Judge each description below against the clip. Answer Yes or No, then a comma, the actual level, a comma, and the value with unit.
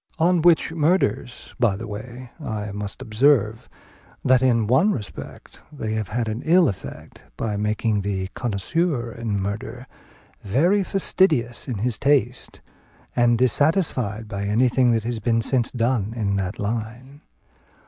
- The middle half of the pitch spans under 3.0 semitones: No, average, 3.7 semitones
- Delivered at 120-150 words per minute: Yes, average, 140 wpm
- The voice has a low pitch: Yes, low, 115 Hz